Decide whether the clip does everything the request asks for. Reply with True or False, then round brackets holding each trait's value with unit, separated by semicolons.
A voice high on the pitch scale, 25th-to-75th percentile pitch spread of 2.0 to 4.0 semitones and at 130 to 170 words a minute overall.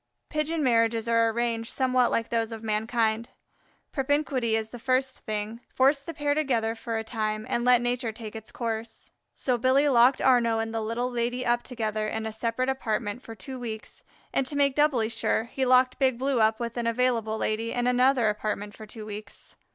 False (235 Hz; 2.5 semitones; 195 wpm)